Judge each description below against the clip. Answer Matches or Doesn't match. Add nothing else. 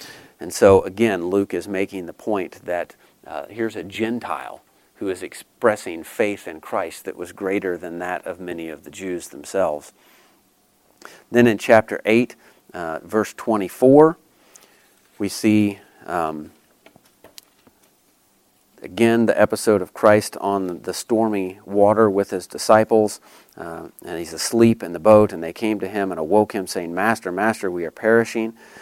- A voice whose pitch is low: Matches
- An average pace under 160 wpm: Matches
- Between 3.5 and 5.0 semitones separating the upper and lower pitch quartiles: Doesn't match